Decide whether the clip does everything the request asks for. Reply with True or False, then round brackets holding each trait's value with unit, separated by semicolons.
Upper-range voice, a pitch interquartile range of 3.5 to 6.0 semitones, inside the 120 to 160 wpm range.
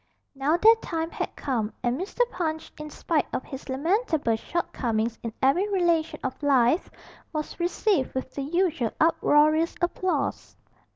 True (310 Hz; 4.6 semitones; 140 wpm)